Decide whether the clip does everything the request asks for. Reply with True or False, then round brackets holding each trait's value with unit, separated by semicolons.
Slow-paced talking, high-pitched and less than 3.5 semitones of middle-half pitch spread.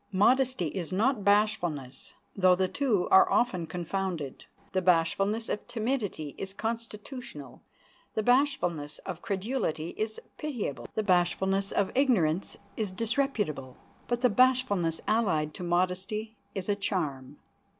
False (125 wpm; 195 Hz; 4.8 semitones)